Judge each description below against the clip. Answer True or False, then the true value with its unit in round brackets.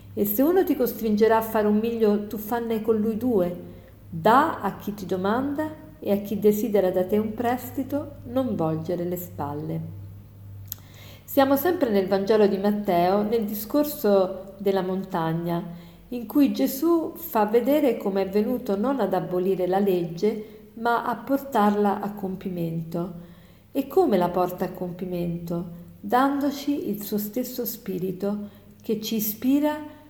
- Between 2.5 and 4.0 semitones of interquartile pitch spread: False (4.9 semitones)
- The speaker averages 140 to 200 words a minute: True (145 wpm)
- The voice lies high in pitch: True (205 Hz)